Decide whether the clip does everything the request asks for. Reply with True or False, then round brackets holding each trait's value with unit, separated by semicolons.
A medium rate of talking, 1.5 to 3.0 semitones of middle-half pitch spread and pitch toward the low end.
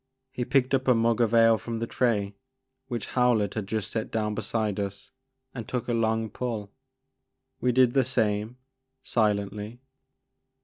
True (160 wpm; 2.5 semitones; 115 Hz)